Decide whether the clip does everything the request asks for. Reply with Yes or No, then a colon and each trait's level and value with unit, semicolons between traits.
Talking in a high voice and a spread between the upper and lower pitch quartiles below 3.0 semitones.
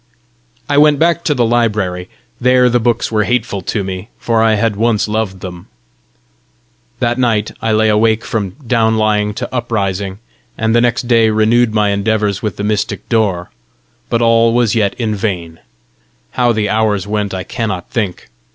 No: low, 110 Hz; narrow, 2.4 semitones